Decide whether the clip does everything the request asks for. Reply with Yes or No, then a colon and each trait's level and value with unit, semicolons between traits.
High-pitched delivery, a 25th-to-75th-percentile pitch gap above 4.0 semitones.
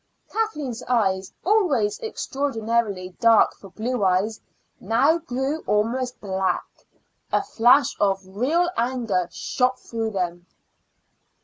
Yes: high, 230 Hz; average, 5.1 semitones